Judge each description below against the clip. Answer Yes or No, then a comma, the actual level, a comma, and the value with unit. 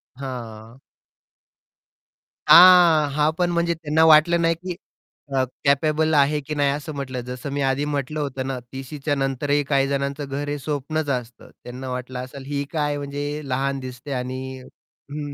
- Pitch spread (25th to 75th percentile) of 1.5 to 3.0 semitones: Yes, narrow, 2.4 semitones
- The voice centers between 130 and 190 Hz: Yes, medium, 140 Hz